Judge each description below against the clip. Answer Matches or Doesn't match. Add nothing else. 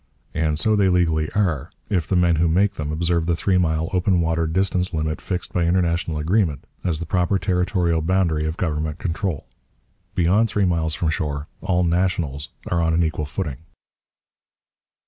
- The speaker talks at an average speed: Matches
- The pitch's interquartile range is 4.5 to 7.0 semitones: Doesn't match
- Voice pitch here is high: Doesn't match